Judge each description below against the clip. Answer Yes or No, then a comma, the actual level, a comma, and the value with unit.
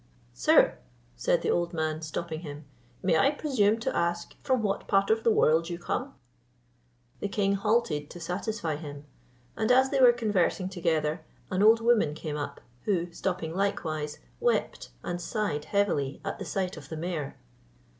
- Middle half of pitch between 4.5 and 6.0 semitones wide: Yes, average, 5.3 semitones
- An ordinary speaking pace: Yes, average, 165 wpm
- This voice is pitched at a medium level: Yes, medium, 175 Hz